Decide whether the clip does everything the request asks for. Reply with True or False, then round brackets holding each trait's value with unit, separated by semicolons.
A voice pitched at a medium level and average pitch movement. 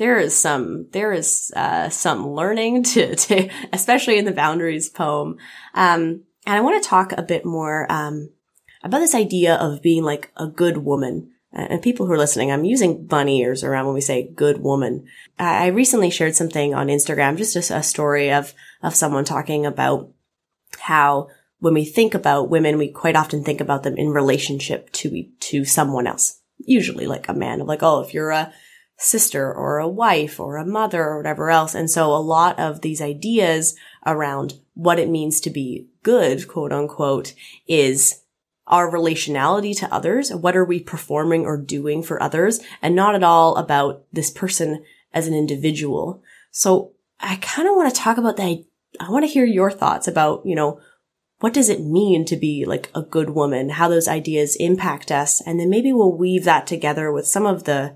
True (160 Hz; 3.8 semitones)